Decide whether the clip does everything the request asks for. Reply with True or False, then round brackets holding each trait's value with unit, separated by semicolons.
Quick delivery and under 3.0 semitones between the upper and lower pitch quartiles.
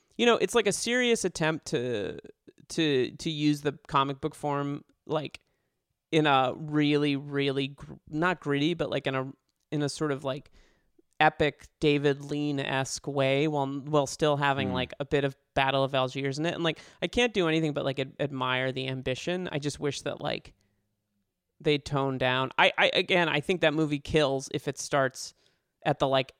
False (190 wpm; 2.5 semitones)